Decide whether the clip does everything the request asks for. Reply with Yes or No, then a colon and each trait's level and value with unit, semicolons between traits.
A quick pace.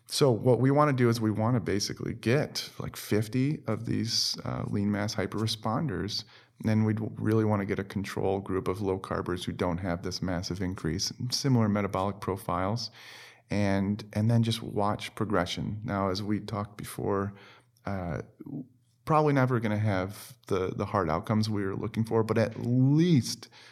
No: average, 175 wpm